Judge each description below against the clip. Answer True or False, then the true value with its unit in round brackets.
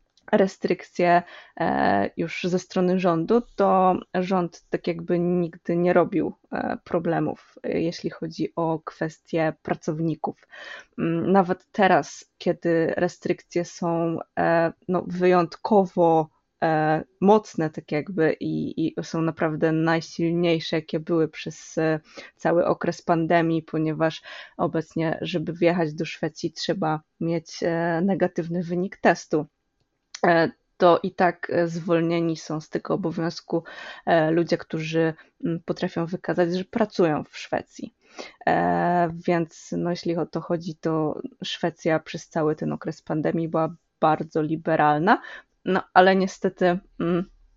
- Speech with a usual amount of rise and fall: False (1.8 semitones)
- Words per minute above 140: False (105 wpm)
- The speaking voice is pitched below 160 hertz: False (170 Hz)